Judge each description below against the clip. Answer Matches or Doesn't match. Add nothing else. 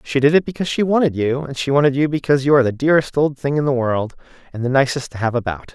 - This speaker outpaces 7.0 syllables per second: Matches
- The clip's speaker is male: Matches